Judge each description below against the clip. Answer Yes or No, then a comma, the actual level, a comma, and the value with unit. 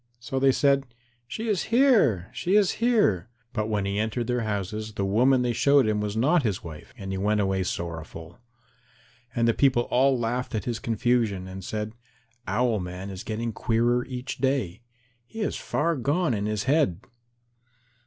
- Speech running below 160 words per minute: No, average, 175 wpm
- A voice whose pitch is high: No, low, 115 Hz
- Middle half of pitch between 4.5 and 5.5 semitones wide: Yes, average, 4.8 semitones